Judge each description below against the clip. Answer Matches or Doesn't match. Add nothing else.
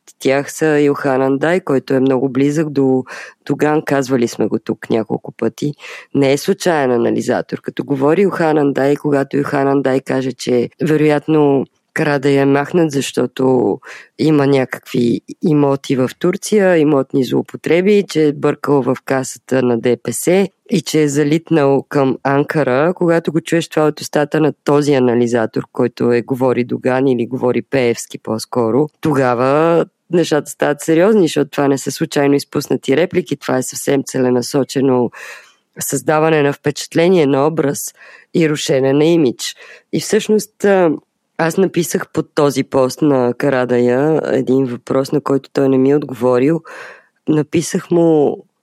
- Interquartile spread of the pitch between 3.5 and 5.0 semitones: Doesn't match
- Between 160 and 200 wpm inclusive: Doesn't match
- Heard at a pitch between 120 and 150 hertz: Matches